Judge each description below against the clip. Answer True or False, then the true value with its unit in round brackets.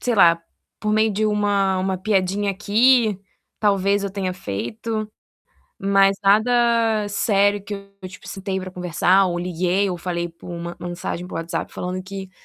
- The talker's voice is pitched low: False (195 Hz)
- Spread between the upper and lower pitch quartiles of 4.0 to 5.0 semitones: False (2.4 semitones)